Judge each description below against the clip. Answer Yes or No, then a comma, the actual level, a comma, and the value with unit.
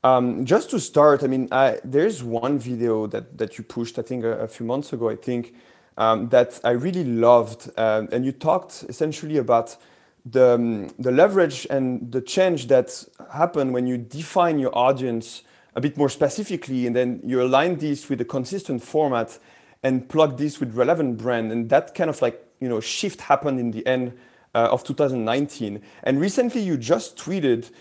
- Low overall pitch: Yes, low, 130 Hz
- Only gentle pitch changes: No, average, 3.5 semitones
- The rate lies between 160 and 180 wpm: No, average, 190 wpm